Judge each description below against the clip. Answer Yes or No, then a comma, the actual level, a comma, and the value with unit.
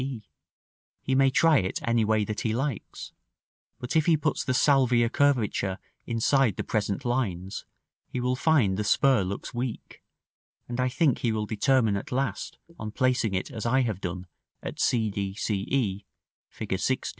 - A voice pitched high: No, low, 120 Hz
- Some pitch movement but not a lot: Yes, average, 4.2 semitones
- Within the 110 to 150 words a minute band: No, average, 170 wpm